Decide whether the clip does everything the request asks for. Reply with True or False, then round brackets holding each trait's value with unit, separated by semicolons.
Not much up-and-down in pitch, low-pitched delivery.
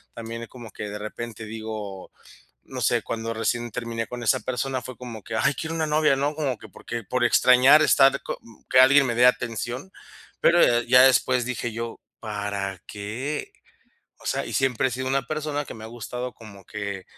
False (3.0 semitones; 120 Hz)